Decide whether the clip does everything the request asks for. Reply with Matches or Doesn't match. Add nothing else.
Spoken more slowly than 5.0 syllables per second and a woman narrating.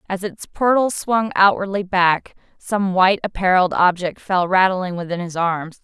Matches